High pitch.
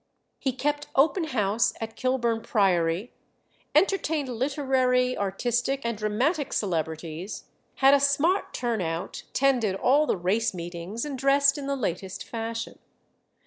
Yes: high, 240 Hz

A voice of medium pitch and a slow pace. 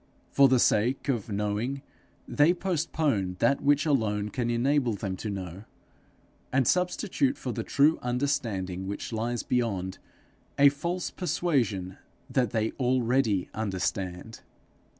No: low, 120 Hz; slow, 125 wpm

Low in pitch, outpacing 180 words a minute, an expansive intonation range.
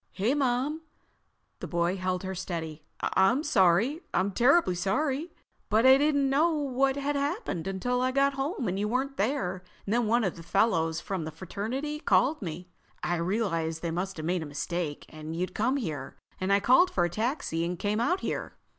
No: high, 205 Hz; average, 190 wpm; wide, 7.6 semitones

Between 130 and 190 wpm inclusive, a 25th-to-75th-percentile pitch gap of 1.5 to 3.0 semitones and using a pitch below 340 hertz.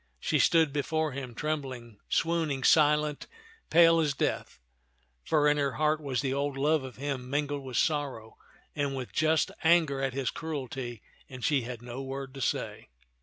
Yes: average, 170 wpm; average, 2.7 semitones; medium, 140 Hz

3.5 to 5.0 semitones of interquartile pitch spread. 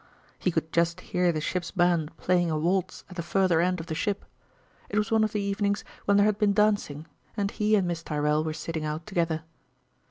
Yes: average, 3.8 semitones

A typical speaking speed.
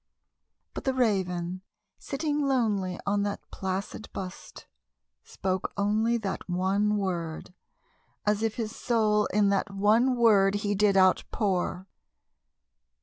No: slow, 115 wpm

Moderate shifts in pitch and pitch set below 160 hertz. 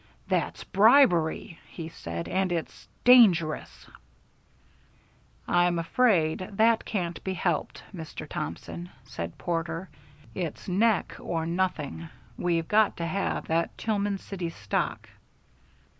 No: average, 3.2 semitones; medium, 175 Hz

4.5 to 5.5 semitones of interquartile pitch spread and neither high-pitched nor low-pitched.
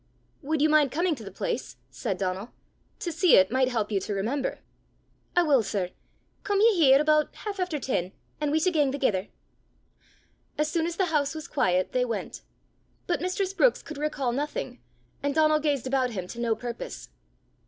No: average, 5.2 semitones; very high, 285 Hz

